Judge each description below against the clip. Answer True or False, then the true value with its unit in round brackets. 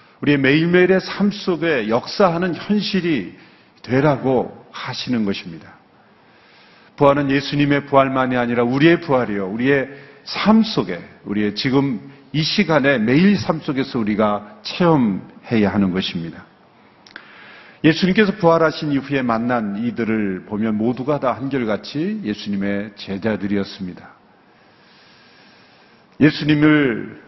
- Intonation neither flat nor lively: False (6.4 semitones)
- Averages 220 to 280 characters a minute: True (275 characters per minute)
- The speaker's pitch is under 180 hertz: True (140 Hz)